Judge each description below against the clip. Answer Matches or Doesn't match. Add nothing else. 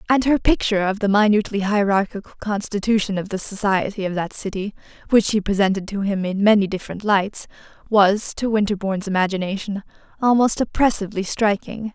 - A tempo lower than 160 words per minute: Matches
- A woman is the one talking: Matches